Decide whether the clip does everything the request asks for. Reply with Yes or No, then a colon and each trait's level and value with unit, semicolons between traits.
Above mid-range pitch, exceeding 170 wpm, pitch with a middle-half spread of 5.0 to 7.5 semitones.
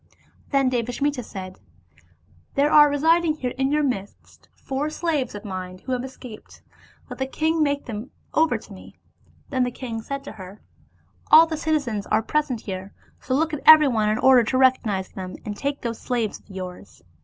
Yes: very high, 255 Hz; average, 190 wpm; wide, 5.4 semitones